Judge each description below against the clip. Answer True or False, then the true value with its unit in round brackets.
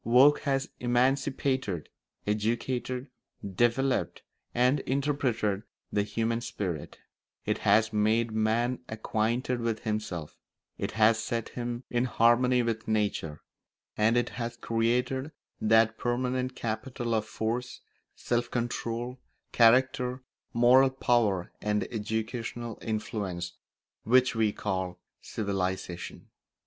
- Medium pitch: False (115 Hz)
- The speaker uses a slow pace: True (105 wpm)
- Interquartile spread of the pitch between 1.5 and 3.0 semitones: True (2.5 semitones)